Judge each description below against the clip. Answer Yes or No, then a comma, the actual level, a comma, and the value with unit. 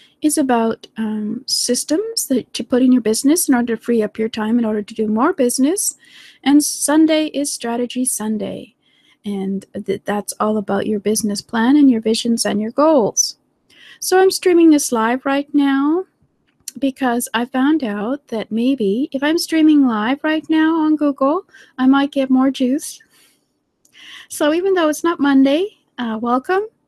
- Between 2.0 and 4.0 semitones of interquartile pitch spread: No, average, 5.1 semitones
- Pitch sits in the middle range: No, very high, 265 Hz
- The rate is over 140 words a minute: Yes, average, 170 wpm